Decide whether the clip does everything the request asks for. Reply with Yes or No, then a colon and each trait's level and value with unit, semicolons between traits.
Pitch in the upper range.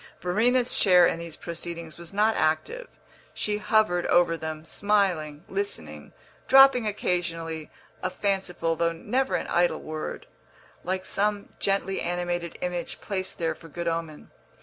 No: medium, 175 Hz